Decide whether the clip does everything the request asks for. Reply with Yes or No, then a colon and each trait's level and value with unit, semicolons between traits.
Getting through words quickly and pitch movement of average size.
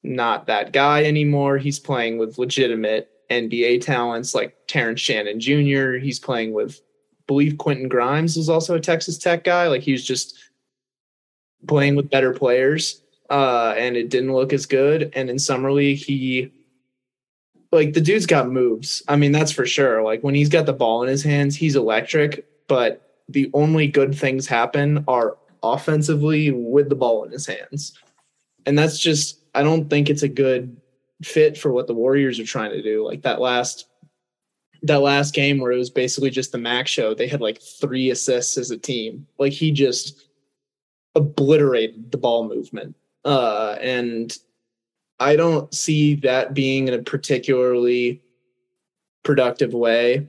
No: average, 170 wpm; average, 3.0 semitones